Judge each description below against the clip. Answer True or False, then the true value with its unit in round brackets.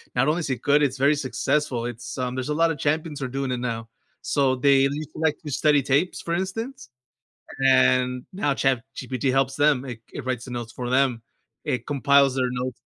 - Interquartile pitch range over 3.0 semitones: False (2.7 semitones)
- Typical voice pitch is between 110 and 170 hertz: True (135 Hz)